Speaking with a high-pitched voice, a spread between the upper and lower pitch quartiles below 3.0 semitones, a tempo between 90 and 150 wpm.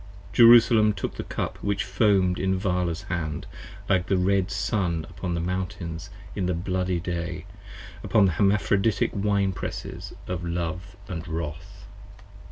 No: very low, 90 Hz; narrow, 2.5 semitones; average, 145 wpm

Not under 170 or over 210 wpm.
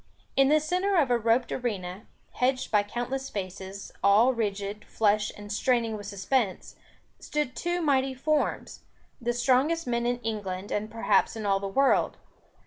No: average, 155 wpm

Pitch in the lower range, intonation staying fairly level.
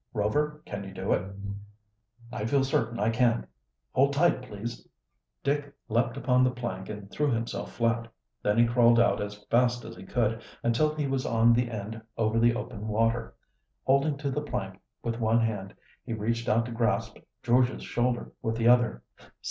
Yes: low, 115 Hz; narrow, 2.2 semitones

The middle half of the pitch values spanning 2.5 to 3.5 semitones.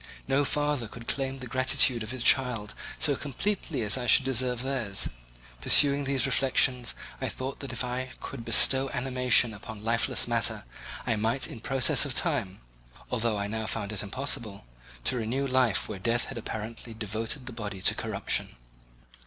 Yes: average, 3.2 semitones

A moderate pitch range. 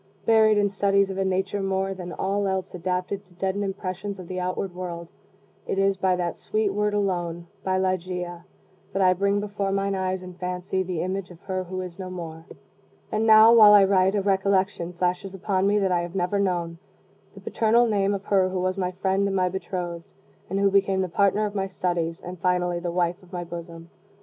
No: narrow, 1.8 semitones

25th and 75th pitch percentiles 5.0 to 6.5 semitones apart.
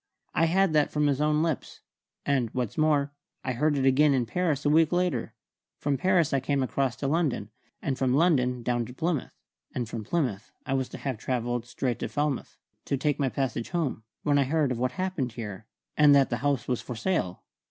No: average, 3.5 semitones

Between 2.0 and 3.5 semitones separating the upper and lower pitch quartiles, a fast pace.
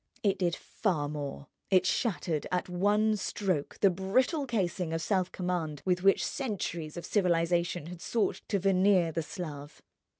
No: average, 3.0 semitones; average, 155 wpm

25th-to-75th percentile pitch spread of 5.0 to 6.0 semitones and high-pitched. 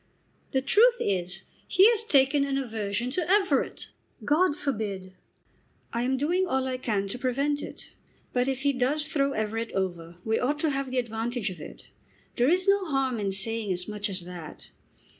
Yes: wide, 5.6 semitones; very high, 255 Hz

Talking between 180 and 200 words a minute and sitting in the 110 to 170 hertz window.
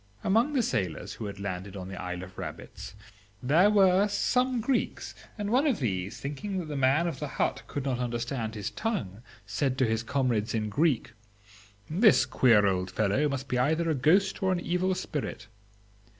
Yes: average, 185 wpm; low, 135 Hz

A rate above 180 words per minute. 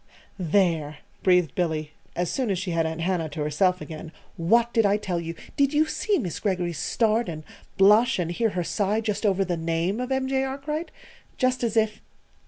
Yes: average, 195 wpm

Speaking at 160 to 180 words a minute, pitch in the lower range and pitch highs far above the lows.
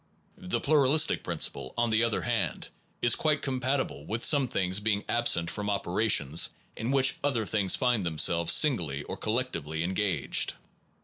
Yes: average, 165 wpm; low, 110 Hz; wide, 6.6 semitones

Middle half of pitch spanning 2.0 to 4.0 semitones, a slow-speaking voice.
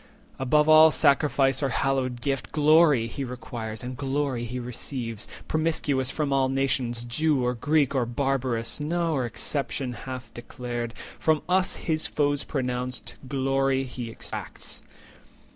Yes: average, 3.0 semitones; slow, 130 wpm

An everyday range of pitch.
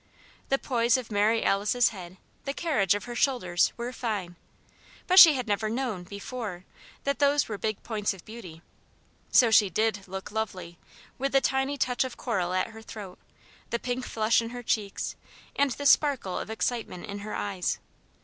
Yes: average, 4.1 semitones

